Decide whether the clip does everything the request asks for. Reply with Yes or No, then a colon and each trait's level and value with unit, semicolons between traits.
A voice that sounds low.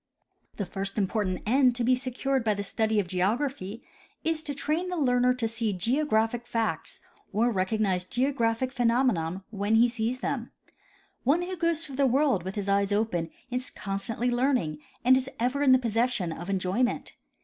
No: high, 235 Hz